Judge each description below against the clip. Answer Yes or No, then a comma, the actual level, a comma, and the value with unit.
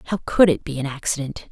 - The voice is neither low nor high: Yes, medium, 155 Hz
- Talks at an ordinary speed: No, fast, 235 wpm